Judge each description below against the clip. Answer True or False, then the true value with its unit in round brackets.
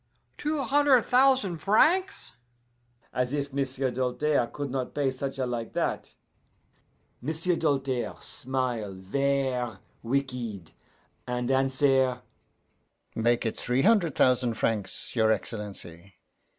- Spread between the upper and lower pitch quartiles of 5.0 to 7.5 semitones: False (3.4 semitones)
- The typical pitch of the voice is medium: False (130 Hz)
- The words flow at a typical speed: False (110 wpm)